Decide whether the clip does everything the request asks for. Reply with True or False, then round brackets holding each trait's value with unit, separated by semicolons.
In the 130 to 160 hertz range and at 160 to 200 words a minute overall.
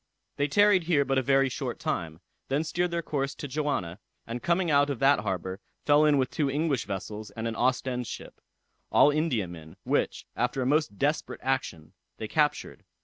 True (135 Hz; 185 wpm)